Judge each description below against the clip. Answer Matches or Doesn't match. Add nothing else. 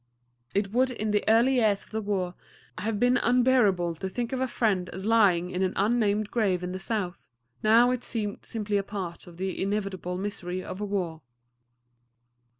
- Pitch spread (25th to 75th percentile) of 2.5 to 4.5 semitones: Matches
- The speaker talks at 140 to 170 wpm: Doesn't match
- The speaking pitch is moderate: Doesn't match